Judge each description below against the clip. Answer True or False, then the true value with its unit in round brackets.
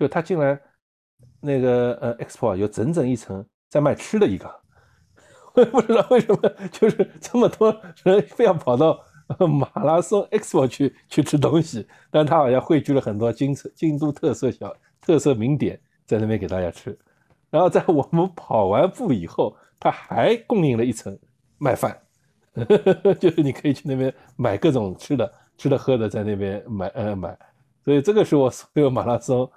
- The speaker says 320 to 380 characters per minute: False (270 characters per minute)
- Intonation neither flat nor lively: False (6.2 semitones)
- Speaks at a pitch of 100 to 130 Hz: False (140 Hz)